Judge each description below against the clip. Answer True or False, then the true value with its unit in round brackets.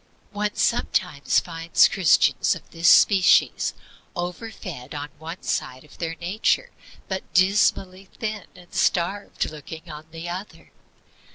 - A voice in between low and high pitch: True (175 Hz)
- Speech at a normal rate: False (125 wpm)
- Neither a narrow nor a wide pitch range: True (3.2 semitones)